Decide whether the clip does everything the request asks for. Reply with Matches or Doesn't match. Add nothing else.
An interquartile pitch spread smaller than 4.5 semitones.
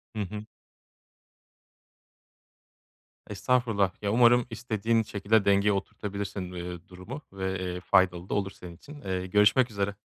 Matches